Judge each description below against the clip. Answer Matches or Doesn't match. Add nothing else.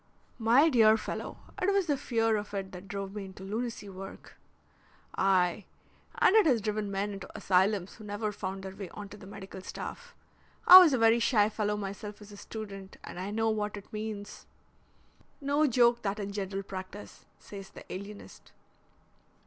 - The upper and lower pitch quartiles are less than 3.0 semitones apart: Matches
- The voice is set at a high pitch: Matches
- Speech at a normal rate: Matches